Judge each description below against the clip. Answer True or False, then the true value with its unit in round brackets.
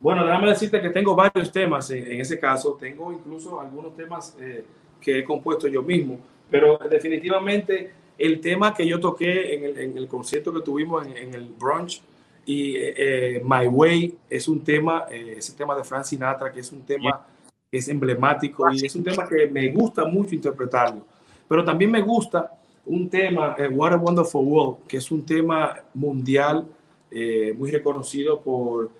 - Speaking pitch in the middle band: True (155 Hz)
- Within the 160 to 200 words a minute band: True (185 wpm)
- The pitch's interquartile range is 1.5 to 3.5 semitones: False (4.2 semitones)